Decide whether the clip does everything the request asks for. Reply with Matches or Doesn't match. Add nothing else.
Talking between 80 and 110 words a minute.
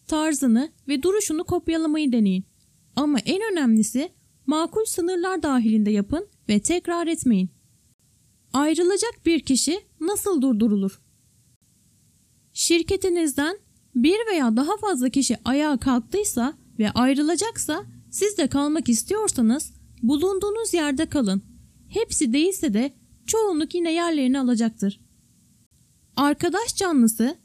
Matches